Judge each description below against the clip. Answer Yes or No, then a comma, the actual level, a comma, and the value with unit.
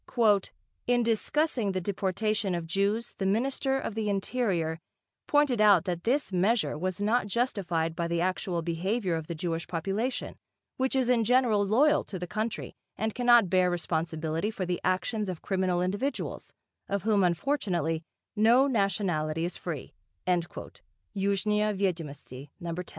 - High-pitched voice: Yes, high, 195 Hz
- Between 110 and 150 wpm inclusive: Yes, average, 145 wpm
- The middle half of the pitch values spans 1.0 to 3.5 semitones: No, average, 4.5 semitones